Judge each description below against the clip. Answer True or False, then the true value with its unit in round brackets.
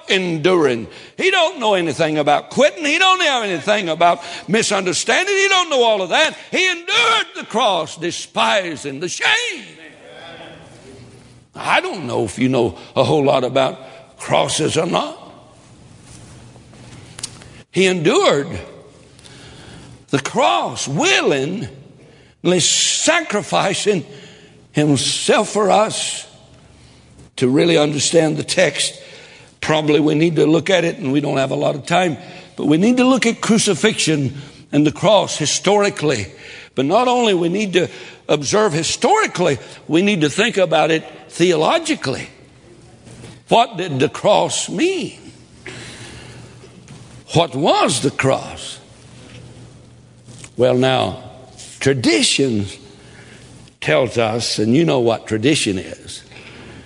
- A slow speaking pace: True (120 wpm)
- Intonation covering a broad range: True (7.1 semitones)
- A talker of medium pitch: True (155 Hz)